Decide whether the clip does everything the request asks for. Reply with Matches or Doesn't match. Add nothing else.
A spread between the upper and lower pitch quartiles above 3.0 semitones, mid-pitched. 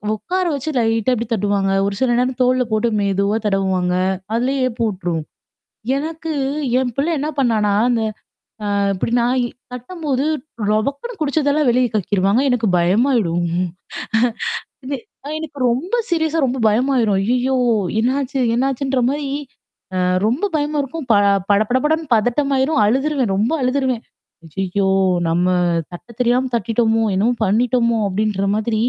Doesn't match